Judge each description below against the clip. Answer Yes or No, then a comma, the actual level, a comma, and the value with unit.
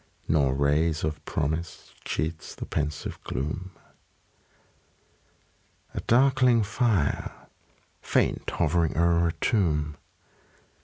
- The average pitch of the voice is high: No, very low, 80 Hz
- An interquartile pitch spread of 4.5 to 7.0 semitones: Yes, average, 4.8 semitones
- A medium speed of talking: No, slow, 90 wpm